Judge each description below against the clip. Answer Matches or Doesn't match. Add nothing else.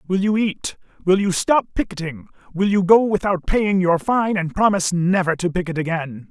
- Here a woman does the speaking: Matches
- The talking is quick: Doesn't match